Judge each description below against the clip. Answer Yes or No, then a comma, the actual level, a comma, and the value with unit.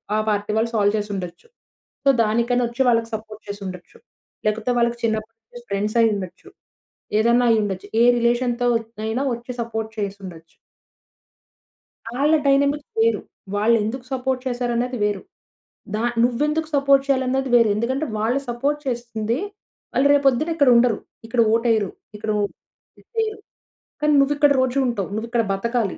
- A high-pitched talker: Yes, high, 235 Hz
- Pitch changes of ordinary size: Yes, average, 3.2 semitones